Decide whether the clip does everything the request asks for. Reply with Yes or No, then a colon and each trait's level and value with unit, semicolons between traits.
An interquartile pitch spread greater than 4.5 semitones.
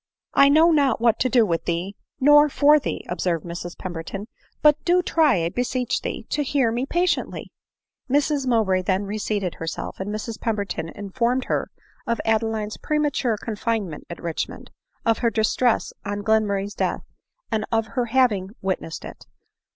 Yes: average, 5.1 semitones